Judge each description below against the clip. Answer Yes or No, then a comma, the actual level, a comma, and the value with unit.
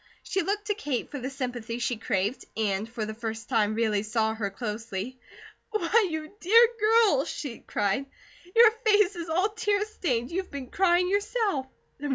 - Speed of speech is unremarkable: Yes, average, 170 wpm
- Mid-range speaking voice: No, very high, 275 Hz